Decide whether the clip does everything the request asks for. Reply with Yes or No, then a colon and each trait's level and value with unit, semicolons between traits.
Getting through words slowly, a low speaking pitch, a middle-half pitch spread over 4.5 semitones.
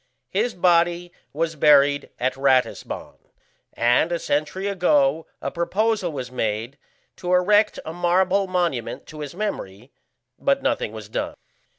No: slow, 130 wpm; medium, 165 Hz; average, 5.3 semitones